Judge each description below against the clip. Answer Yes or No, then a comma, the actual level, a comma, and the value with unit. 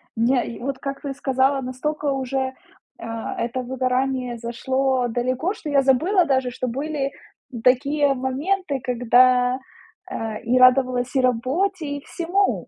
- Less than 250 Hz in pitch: No, very high, 260 Hz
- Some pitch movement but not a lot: No, narrow, 2.2 semitones